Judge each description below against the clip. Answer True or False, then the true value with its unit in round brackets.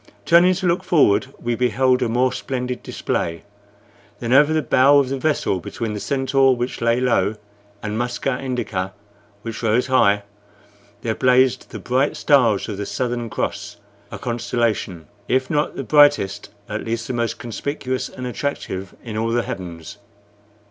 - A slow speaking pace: False (160 wpm)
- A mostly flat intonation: False (3.0 semitones)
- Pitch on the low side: True (125 Hz)